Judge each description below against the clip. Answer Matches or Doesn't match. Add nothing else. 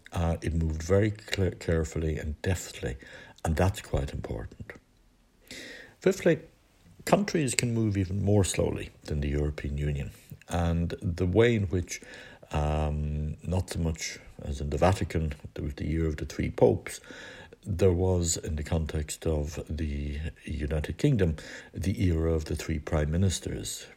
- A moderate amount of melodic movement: Matches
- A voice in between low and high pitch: Doesn't match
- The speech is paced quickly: Doesn't match